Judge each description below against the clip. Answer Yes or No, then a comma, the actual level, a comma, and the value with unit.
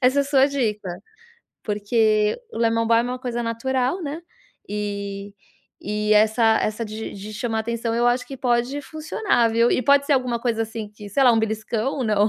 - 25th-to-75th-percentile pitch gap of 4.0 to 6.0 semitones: No, average, 2.9 semitones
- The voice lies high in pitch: Yes, high, 230 Hz